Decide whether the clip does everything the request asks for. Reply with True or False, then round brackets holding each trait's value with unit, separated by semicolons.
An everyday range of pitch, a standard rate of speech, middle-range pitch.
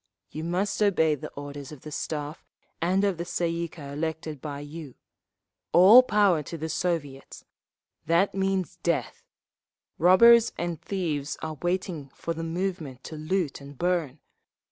True (3.7 semitones; 145 wpm; 165 Hz)